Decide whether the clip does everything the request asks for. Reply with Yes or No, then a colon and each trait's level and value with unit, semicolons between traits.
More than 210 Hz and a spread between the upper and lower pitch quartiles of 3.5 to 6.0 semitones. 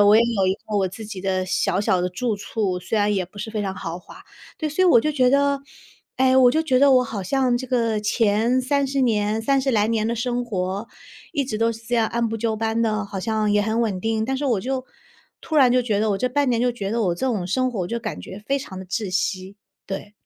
Yes: high, 225 Hz; average, 3.8 semitones